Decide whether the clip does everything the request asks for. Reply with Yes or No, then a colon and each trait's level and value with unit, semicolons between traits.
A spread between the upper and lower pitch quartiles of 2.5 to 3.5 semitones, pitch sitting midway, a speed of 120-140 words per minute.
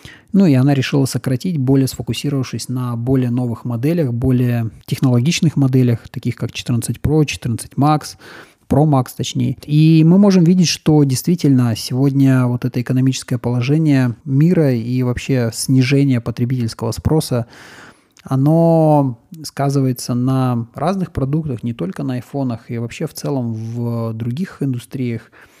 No: average, 2.8 semitones; low, 130 Hz; average, 130 wpm